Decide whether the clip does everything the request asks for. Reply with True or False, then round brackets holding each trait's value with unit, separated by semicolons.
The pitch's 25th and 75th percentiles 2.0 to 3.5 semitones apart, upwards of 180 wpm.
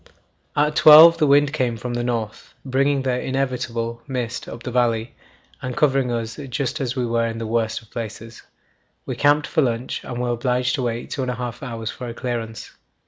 True (2.5 semitones; 200 wpm)